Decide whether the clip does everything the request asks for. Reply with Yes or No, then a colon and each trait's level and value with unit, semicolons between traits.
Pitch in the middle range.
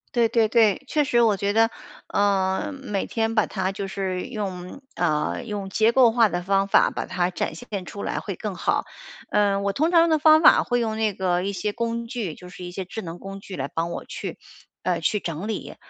No: high, 200 Hz